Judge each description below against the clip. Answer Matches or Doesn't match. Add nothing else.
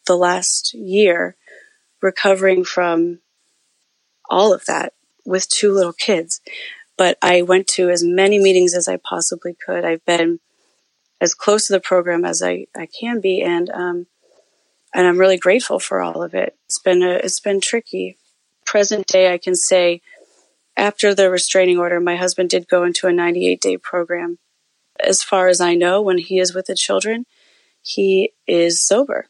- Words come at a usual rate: Matches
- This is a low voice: Doesn't match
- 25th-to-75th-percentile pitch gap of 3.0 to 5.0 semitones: Doesn't match